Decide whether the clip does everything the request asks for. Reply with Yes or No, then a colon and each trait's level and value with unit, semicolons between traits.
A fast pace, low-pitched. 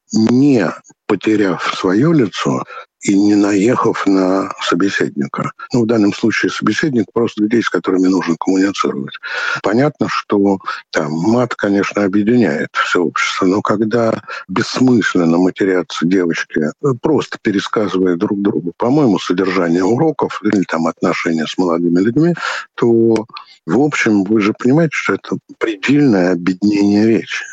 No: average, 125 wpm; low, 105 Hz